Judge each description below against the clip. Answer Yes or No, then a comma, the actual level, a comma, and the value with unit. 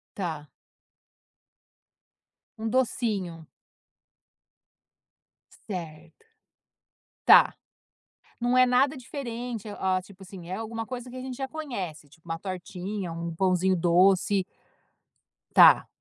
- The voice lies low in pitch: No, high, 195 Hz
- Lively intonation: Yes, wide, 5.7 semitones